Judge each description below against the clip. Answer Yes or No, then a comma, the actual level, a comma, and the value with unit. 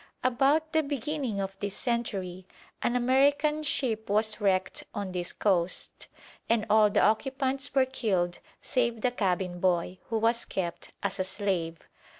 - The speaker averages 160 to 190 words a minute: No, average, 150 wpm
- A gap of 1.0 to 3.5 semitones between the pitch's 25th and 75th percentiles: No, wide, 5.5 semitones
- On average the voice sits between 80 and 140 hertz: No, high, 215 Hz